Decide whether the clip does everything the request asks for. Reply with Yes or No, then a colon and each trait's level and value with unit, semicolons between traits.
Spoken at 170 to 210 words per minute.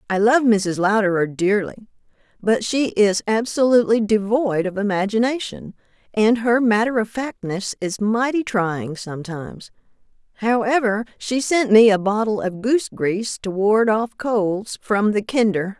No: average, 140 wpm